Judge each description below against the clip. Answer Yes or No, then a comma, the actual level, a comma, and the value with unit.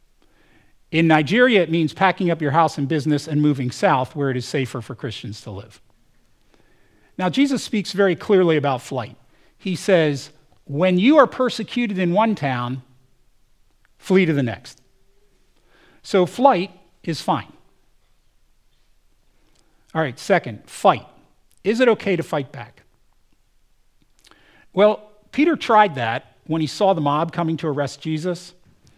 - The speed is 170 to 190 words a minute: No, average, 140 wpm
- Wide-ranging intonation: Yes, wide, 6.2 semitones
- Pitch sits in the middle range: Yes, medium, 160 Hz